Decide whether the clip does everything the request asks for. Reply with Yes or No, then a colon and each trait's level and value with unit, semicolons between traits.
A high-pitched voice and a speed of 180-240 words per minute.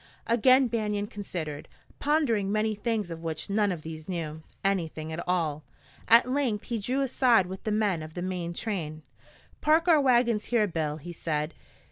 No: high, 200 Hz; average, 170 wpm